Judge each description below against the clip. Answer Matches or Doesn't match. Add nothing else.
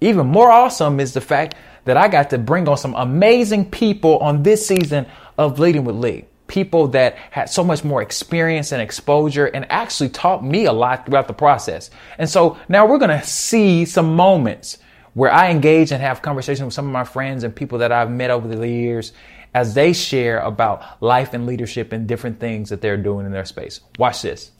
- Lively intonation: Matches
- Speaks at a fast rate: Matches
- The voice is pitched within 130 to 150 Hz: Matches